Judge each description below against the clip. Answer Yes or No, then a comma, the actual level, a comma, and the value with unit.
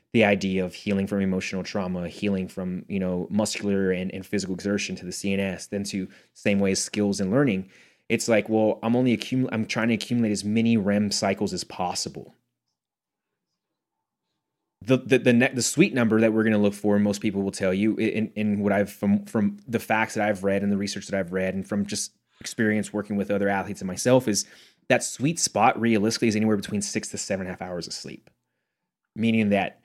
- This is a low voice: Yes, low, 100 Hz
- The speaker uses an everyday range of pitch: No, narrow, 2.0 semitones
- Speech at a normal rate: No, fast, 215 wpm